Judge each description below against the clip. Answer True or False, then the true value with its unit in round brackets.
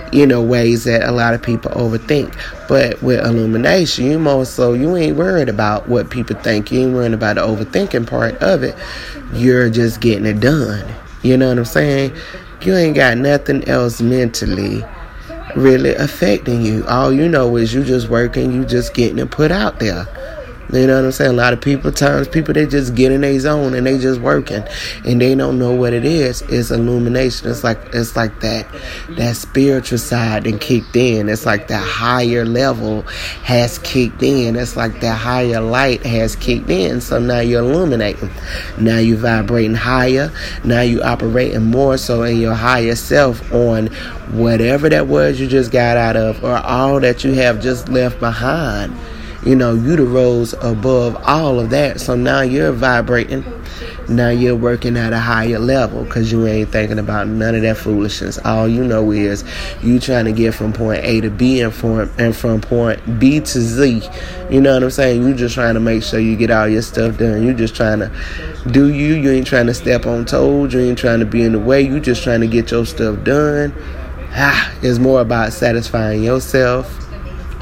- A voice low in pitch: True (120 Hz)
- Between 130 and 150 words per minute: False (200 wpm)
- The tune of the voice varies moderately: False (2.3 semitones)